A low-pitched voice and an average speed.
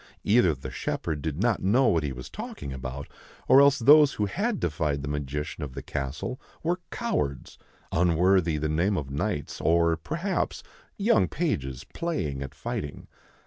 Yes: very low, 80 Hz; average, 160 wpm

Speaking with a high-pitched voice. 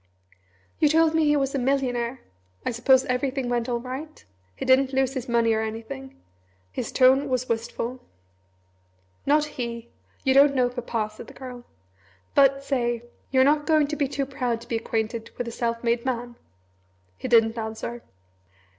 Yes: very high, 250 Hz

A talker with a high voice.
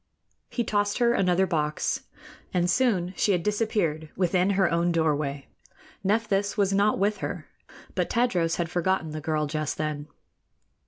No: medium, 180 Hz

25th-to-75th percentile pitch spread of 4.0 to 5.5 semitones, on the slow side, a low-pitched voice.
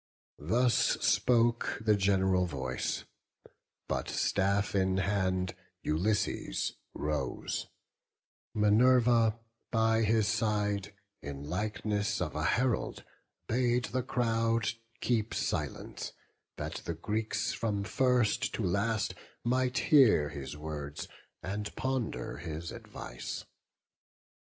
Yes: average, 4.3 semitones; slow, 100 wpm; low, 105 Hz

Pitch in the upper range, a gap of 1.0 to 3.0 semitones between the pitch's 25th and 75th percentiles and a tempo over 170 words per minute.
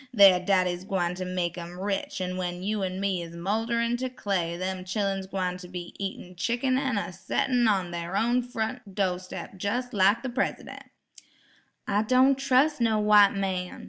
No: high, 195 Hz; average, 4.2 semitones; average, 180 wpm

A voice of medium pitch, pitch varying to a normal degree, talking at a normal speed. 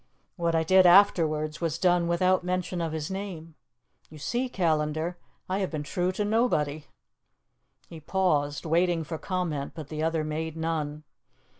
Yes: medium, 165 Hz; average, 3.0 semitones; average, 155 wpm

